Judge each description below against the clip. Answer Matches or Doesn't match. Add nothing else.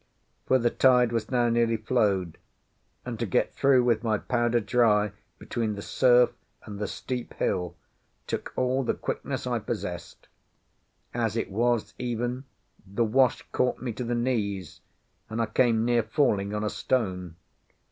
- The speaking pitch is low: Matches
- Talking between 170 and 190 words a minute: Doesn't match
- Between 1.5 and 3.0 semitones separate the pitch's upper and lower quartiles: Matches